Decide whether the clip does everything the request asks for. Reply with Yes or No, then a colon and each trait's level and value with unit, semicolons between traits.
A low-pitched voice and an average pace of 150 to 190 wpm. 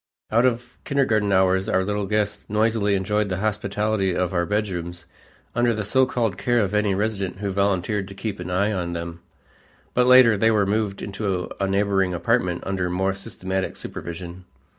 Yes: low, 100 Hz; average, 175 wpm